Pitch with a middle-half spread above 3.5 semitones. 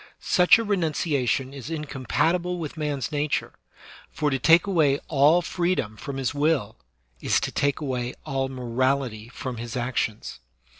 Yes: average, 4.0 semitones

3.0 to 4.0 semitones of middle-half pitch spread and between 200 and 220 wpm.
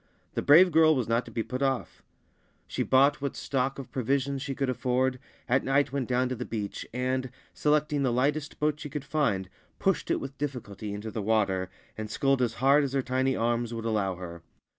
Yes: average, 3.3 semitones; fast, 205 wpm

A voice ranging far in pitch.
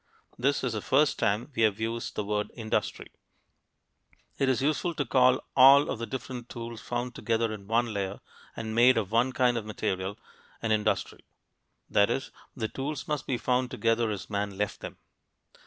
No: average, 3.1 semitones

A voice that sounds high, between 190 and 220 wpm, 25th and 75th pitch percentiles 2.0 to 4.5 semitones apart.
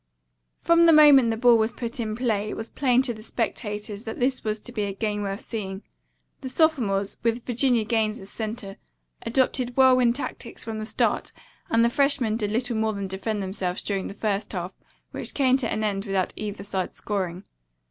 Yes: high, 220 Hz; average, 200 wpm; average, 3.3 semitones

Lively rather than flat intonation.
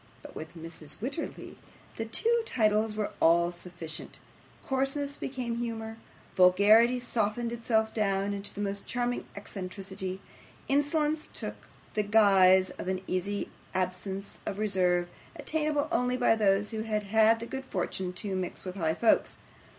No: average, 4.2 semitones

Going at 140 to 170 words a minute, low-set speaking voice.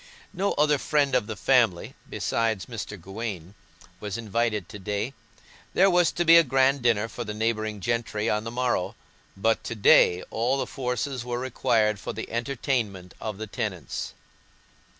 Yes: average, 165 wpm; low, 115 Hz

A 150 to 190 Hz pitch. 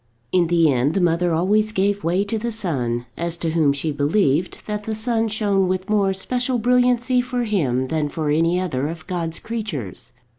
Yes: medium, 185 Hz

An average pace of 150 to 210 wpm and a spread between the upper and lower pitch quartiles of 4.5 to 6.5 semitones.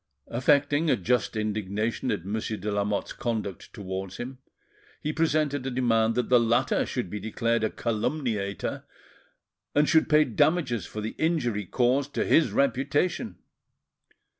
No: average, 140 wpm; average, 5.0 semitones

